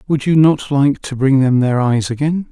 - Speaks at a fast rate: Yes, fast, 240 wpm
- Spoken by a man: Yes, male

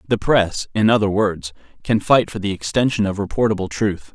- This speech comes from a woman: No, male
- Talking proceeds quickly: No, average, 190 wpm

